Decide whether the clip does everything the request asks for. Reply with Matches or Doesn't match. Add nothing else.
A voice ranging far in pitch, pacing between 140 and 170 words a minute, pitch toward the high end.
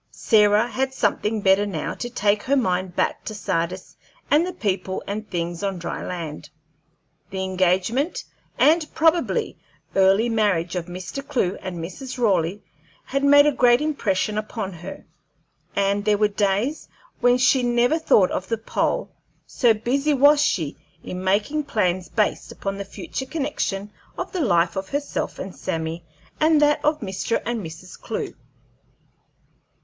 Matches